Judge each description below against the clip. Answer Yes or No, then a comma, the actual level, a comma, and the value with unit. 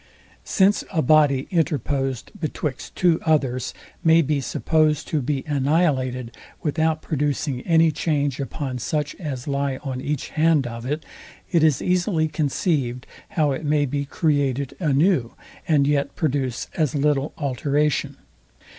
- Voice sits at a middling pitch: Yes, medium, 145 Hz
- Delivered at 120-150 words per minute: Yes, slow, 135 wpm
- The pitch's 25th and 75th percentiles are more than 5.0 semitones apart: No, average, 2.7 semitones